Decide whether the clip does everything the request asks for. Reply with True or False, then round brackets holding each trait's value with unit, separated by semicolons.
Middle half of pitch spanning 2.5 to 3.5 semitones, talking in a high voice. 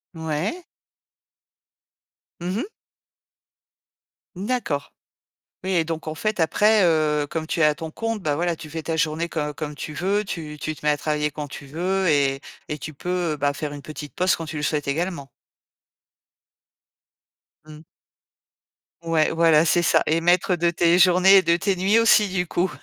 False (3.2 semitones; 165 Hz)